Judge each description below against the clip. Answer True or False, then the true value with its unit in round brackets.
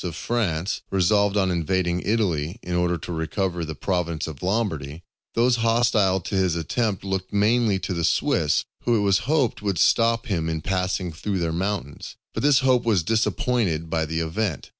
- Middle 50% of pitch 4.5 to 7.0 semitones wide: True (4.8 semitones)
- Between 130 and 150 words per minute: False (180 wpm)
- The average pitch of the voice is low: True (95 Hz)